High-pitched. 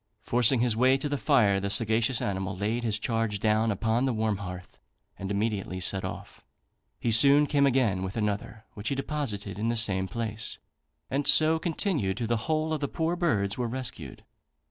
No: low, 115 Hz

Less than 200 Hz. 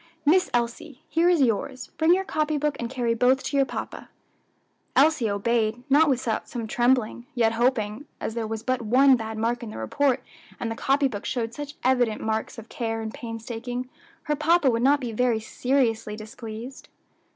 No: high, 245 Hz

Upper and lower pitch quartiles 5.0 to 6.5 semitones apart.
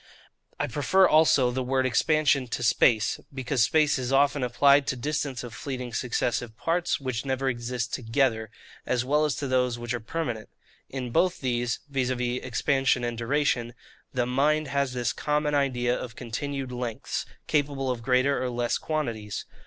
No: average, 2.7 semitones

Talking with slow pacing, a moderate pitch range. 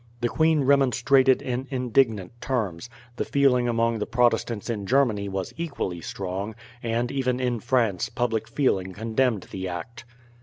No: average, 145 wpm; average, 4.0 semitones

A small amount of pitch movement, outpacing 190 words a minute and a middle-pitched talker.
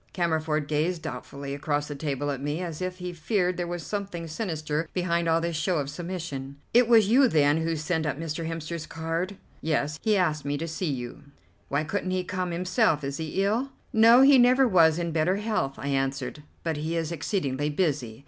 No: average, 3.6 semitones; average, 200 wpm; medium, 165 Hz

